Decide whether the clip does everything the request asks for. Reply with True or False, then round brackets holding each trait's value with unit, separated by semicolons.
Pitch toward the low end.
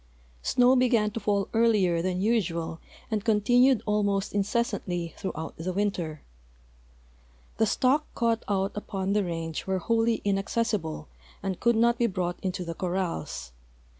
False (200 Hz)